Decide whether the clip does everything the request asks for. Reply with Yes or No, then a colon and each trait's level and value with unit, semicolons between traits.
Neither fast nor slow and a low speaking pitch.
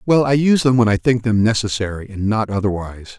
No: fast, 225 wpm; low, 110 Hz